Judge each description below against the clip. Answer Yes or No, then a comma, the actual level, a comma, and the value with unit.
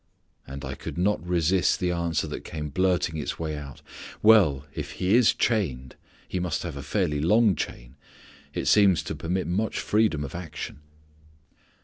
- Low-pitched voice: Yes, very low, 85 Hz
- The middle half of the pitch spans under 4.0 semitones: No, average, 4.4 semitones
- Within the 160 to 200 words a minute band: Yes, average, 165 wpm